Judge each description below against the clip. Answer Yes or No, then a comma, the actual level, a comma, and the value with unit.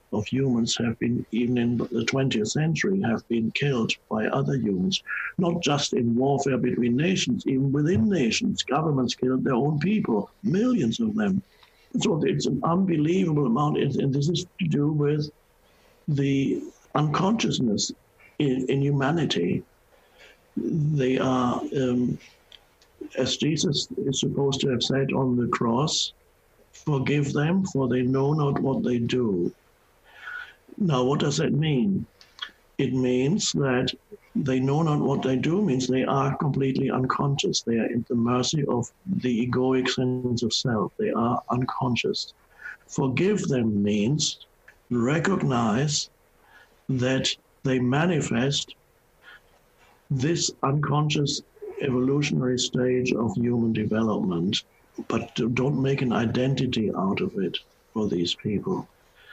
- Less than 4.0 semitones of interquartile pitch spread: Yes, average, 3.4 semitones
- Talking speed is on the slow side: Yes, slow, 130 wpm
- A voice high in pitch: No, low, 135 Hz